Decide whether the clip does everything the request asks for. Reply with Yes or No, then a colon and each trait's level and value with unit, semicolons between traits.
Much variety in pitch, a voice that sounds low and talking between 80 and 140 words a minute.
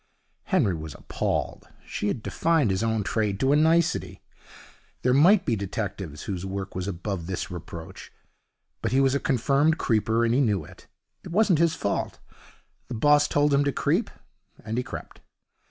No: wide, 6.9 semitones; low, 115 Hz; average, 170 wpm